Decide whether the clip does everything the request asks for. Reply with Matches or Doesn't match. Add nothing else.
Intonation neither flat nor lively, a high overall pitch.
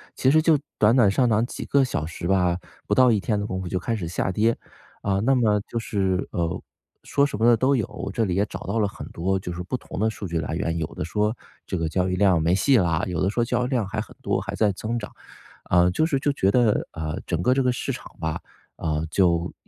Doesn't match